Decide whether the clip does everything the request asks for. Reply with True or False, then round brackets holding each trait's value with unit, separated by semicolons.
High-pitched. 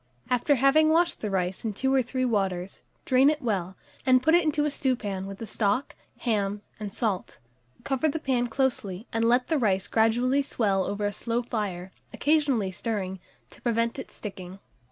True (230 Hz)